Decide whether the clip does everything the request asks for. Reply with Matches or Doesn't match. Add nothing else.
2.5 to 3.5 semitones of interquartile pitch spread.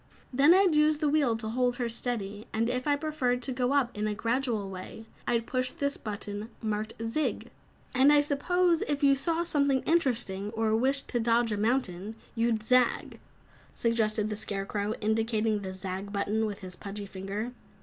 Doesn't match